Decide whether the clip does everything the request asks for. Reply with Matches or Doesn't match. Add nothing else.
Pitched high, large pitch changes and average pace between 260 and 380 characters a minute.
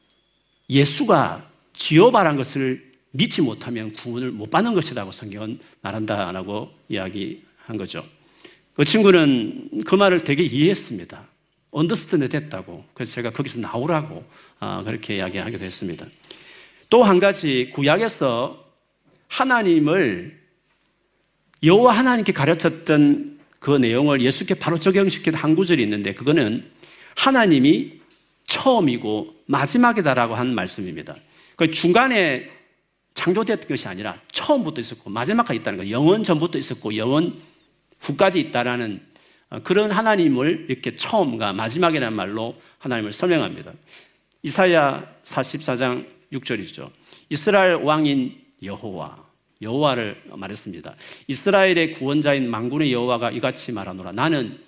Doesn't match